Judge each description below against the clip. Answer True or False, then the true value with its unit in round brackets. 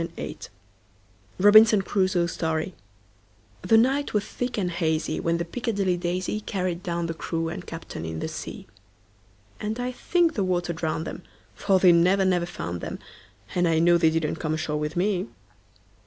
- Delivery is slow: False (150 wpm)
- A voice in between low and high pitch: True (175 Hz)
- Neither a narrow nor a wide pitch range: True (3.4 semitones)